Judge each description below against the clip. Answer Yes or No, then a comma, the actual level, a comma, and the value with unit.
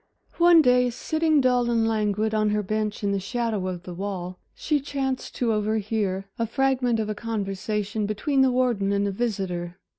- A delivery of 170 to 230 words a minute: Yes, average, 180 wpm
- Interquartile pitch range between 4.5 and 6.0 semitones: No, average, 3.8 semitones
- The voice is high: Yes, high, 215 Hz